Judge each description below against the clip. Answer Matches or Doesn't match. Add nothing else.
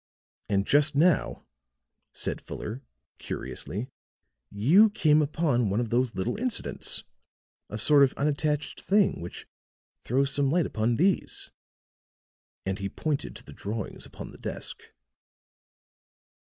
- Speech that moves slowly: Matches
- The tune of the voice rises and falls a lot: Matches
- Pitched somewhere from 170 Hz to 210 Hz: Doesn't match